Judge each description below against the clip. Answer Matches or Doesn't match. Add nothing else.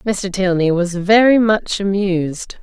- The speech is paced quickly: Doesn't match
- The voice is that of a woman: Matches